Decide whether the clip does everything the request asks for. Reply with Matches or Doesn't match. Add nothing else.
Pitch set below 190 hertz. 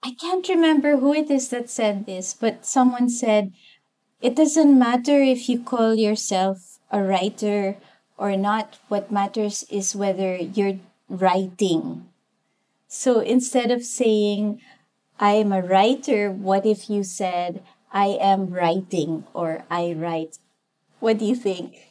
Doesn't match